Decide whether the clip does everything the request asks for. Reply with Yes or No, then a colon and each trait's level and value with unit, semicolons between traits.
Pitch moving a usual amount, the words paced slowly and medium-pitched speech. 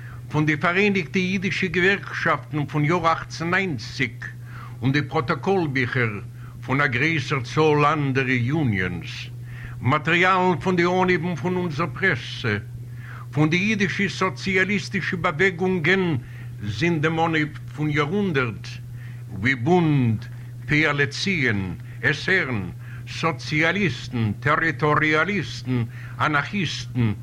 No: wide, 6.3 semitones; slow, 90 wpm; medium, 145 Hz